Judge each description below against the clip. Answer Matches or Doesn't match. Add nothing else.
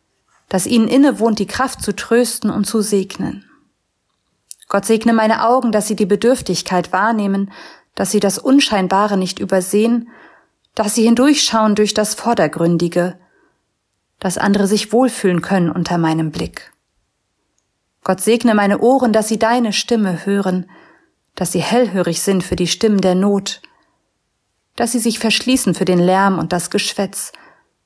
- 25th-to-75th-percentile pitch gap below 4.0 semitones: Matches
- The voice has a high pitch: Matches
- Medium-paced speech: Matches